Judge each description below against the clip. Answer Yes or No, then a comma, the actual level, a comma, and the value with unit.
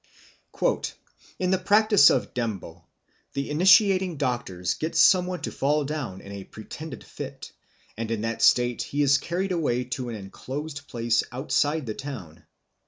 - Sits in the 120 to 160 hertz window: Yes, medium, 140 Hz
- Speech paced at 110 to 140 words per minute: No, average, 160 wpm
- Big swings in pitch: Yes, wide, 6.3 semitones